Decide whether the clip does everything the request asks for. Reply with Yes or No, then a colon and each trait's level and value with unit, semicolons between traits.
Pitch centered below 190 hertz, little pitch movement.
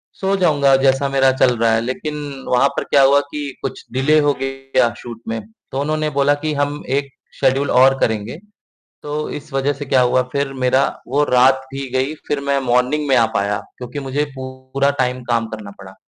Yes: low, 135 Hz; narrow, 2.3 semitones